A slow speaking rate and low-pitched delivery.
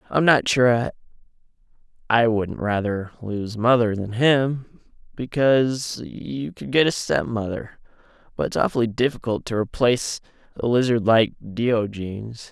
Yes: slow, 130 wpm; low, 115 Hz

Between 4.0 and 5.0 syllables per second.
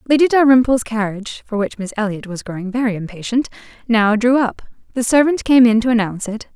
No: 6.0 syllables/s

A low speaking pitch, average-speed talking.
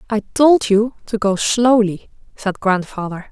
No: high, 210 Hz; average, 145 wpm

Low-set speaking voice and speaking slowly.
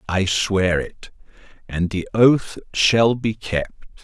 Yes: low, 100 Hz; slow, 120 wpm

